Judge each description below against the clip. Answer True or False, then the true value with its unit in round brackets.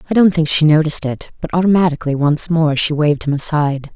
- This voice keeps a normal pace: False (210 wpm)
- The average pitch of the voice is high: False (155 Hz)